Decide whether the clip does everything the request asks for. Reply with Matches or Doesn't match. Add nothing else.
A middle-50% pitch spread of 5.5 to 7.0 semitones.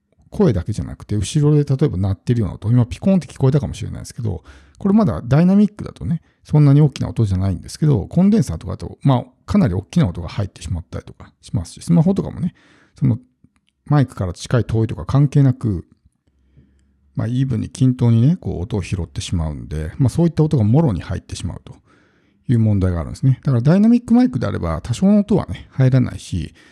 Doesn't match